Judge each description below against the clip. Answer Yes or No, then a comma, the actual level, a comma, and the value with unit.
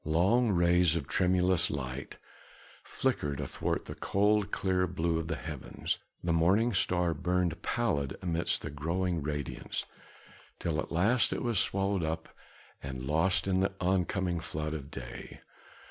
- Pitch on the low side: Yes, very low, 85 Hz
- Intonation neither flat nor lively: Yes, average, 3.4 semitones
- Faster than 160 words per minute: No, average, 145 wpm